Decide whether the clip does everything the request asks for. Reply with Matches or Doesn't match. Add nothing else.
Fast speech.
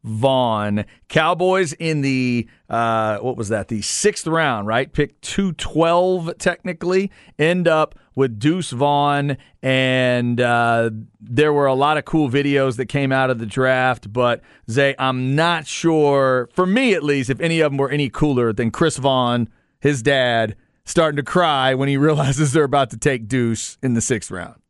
Doesn't match